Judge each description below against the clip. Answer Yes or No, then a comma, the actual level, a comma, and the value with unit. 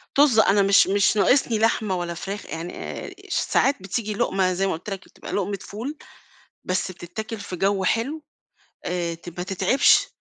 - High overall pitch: Yes, high, 195 Hz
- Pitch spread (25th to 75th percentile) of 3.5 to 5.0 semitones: No, average, 3.1 semitones